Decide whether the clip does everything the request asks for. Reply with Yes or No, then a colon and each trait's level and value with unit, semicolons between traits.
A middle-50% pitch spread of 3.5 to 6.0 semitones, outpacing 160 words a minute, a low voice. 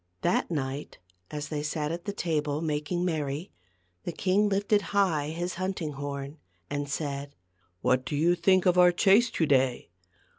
No: average, 3.9 semitones; average, 170 wpm; medium, 155 Hz